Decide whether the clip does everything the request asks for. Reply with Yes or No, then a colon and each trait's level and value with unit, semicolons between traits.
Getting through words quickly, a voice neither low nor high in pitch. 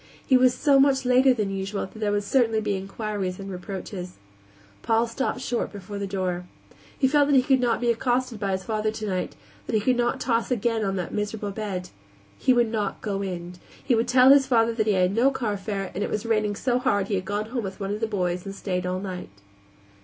No: fast, 230 wpm; high, 215 Hz